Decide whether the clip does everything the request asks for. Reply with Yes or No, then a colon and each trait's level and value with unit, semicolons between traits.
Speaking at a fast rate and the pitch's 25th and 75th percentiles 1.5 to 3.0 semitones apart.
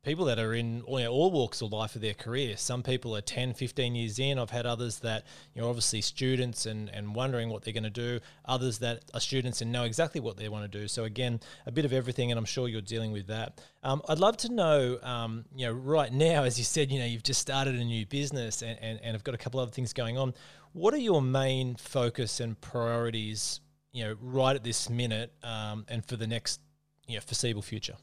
Yes: fast, 250 wpm; narrow, 2.6 semitones